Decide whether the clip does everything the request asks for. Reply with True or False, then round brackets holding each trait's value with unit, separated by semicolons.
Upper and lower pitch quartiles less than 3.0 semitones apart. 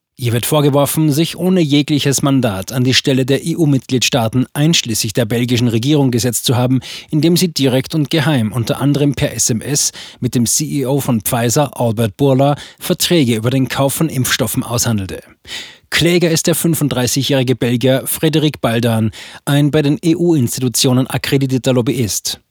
False (3.4 semitones)